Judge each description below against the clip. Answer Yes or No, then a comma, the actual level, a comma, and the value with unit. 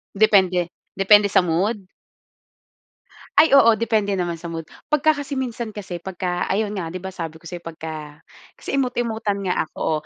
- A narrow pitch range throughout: No, average, 4.3 semitones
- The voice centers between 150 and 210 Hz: Yes, high, 190 Hz